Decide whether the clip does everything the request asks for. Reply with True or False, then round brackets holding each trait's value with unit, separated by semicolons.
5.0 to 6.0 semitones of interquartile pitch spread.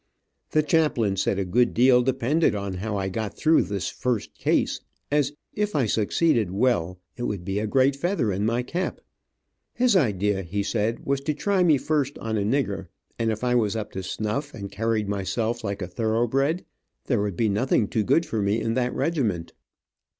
True (5.3 semitones)